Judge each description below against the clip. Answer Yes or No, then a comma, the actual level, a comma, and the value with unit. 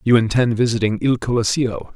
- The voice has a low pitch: Yes, low, 115 Hz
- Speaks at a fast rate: No, average, 155 wpm